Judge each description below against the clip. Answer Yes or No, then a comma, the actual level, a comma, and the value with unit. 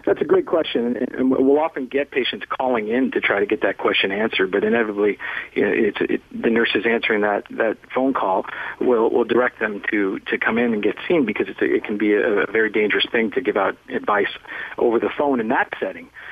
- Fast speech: Yes, fast, 230 wpm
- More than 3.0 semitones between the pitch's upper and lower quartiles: Yes, average, 4.1 semitones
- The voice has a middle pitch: No, low, 125 Hz